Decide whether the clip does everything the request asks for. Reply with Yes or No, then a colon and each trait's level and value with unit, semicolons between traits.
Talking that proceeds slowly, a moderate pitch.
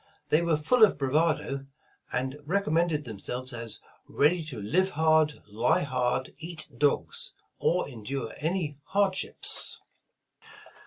Yes: slow, 120 wpm; medium, 150 Hz